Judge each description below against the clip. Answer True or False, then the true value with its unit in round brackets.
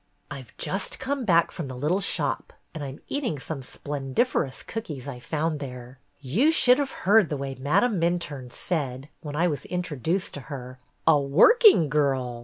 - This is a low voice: False (150 Hz)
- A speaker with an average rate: True (180 wpm)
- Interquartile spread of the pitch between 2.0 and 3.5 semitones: False (5.3 semitones)